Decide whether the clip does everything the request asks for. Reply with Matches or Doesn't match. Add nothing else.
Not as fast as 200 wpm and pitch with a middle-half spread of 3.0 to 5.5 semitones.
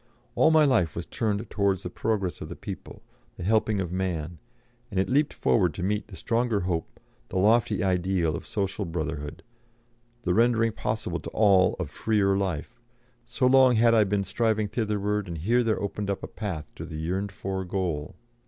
Matches